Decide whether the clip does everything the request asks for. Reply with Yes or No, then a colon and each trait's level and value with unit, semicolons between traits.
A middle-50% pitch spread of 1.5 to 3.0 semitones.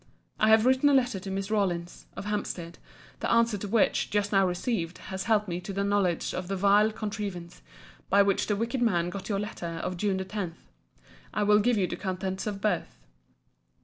Yes: narrow, 2.5 semitones